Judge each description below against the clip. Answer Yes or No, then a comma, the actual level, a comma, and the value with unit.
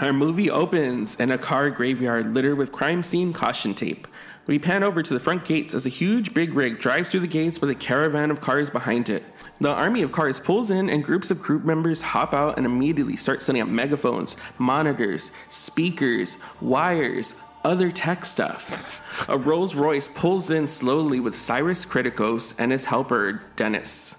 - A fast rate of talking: No, average, 185 wpm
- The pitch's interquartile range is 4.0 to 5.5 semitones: Yes, average, 5.0 semitones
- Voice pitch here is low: No, medium, 150 Hz